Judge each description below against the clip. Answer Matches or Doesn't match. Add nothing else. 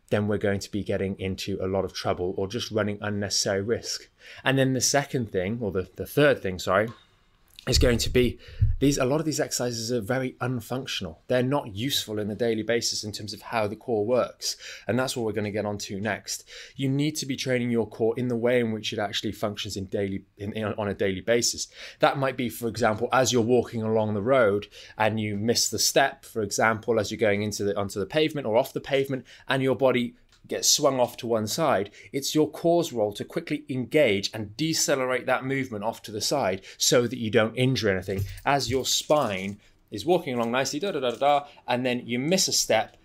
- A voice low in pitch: Matches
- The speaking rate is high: Matches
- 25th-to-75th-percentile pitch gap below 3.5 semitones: Doesn't match